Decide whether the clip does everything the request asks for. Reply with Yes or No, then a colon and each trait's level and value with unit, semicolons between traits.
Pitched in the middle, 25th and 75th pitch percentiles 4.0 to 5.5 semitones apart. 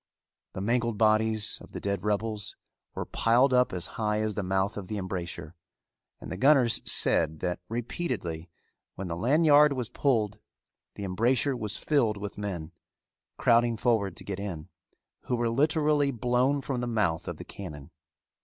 No: low, 110 Hz; average, 4.3 semitones